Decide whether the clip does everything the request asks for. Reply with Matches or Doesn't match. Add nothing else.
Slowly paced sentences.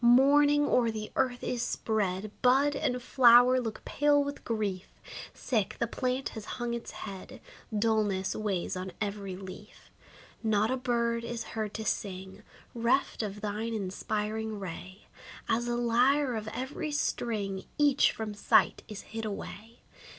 Doesn't match